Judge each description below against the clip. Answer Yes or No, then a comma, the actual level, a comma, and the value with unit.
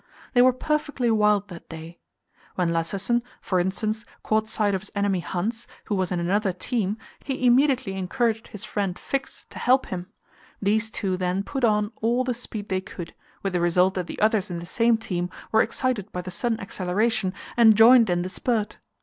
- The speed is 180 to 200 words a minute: Yes, average, 190 wpm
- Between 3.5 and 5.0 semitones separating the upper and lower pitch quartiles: Yes, average, 4.0 semitones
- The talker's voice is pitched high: Yes, high, 210 Hz